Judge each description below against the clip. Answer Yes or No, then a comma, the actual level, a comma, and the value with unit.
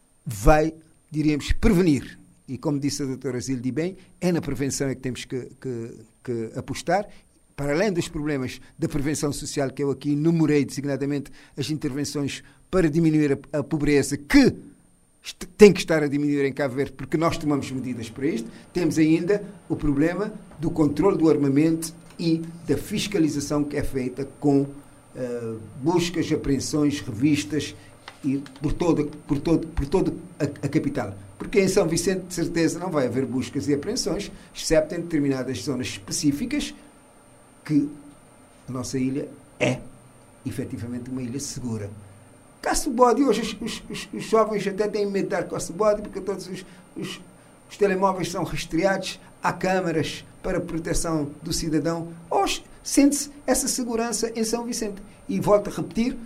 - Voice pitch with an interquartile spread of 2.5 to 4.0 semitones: No, average, 4.6 semitones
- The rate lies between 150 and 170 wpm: Yes, average, 155 wpm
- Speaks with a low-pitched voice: No, medium, 150 Hz